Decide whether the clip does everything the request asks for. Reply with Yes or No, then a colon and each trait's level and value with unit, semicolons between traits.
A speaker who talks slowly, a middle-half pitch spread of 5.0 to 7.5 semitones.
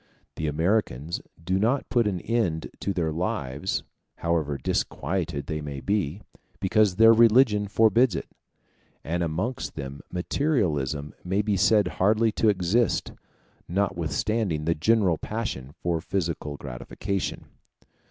Yes: slow, 125 wpm; wide, 5.5 semitones